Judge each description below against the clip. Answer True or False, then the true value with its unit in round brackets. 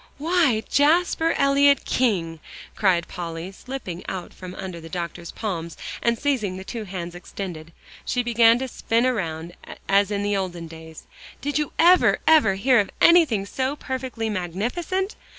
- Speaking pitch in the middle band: False (210 Hz)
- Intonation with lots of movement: True (7.1 semitones)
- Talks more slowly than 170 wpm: True (150 wpm)